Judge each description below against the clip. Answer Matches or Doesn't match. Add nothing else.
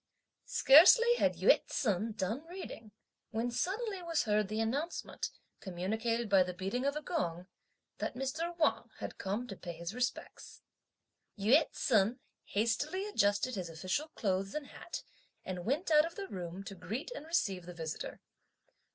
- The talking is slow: Doesn't match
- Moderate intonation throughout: Doesn't match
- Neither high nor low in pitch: Doesn't match